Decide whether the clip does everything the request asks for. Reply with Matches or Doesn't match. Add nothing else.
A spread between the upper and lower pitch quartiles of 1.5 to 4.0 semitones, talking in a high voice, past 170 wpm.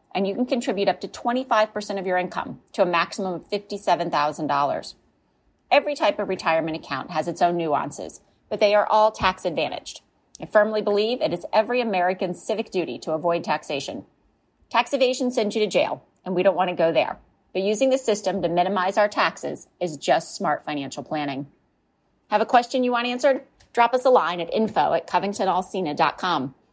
Doesn't match